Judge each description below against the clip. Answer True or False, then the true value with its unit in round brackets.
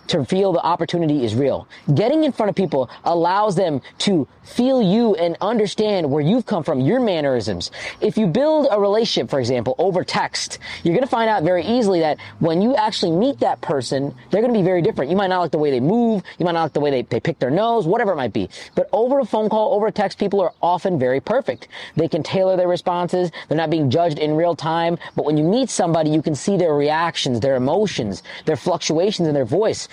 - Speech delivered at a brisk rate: True (235 wpm)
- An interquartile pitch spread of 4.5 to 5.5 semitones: True (4.8 semitones)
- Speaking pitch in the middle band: True (175 Hz)